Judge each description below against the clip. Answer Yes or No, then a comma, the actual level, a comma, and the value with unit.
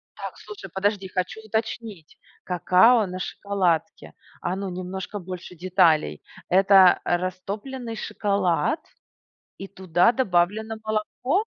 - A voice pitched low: No, high, 190 Hz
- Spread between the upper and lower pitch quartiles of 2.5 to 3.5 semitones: Yes, average, 3.2 semitones